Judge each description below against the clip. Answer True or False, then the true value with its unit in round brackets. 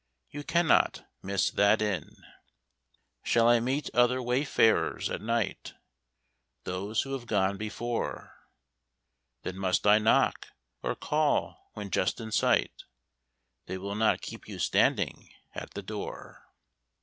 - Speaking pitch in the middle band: False (110 Hz)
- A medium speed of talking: False (125 wpm)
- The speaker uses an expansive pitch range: False (3.5 semitones)